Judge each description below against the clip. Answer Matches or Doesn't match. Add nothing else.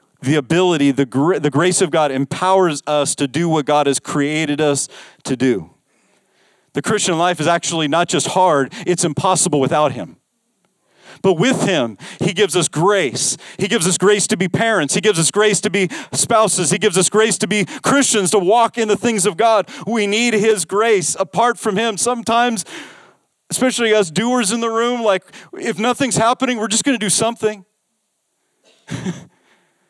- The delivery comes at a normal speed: Matches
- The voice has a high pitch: Matches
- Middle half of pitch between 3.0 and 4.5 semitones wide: Doesn't match